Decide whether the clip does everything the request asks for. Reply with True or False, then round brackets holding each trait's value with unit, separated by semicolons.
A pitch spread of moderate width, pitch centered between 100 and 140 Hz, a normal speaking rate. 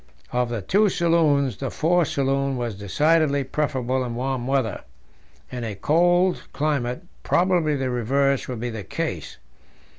True (4.1 semitones; 135 Hz; 145 wpm)